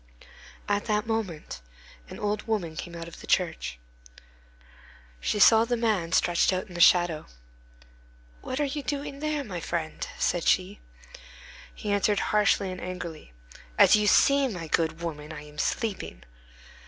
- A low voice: No, medium, 185 Hz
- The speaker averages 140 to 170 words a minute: Yes, average, 155 wpm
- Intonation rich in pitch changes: No, average, 4.8 semitones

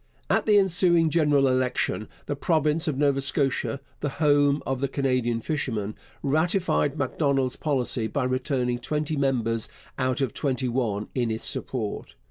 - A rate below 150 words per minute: Yes, average, 140 wpm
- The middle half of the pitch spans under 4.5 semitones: Yes, average, 2.9 semitones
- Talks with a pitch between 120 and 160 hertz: Yes, low, 135 Hz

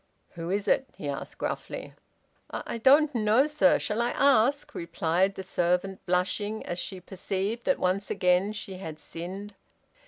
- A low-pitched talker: No, high, 195 Hz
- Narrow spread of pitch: No, average, 4.3 semitones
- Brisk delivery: No, average, 160 wpm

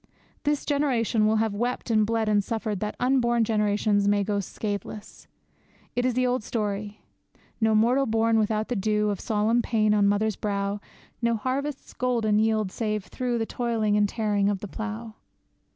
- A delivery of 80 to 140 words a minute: No, average, 170 wpm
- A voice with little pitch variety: Yes, narrow, 2.1 semitones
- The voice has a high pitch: Yes, high, 220 Hz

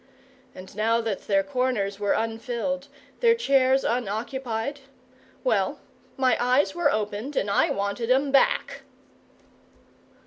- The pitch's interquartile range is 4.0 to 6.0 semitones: Yes, average, 4.4 semitones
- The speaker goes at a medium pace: No, slow, 115 wpm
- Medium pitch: No, high, 240 Hz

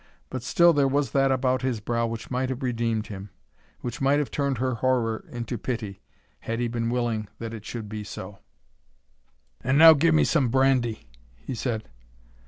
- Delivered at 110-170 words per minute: No, average, 180 wpm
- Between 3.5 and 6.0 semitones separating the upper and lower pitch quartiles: No, average, 2.8 semitones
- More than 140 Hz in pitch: No, low, 120 Hz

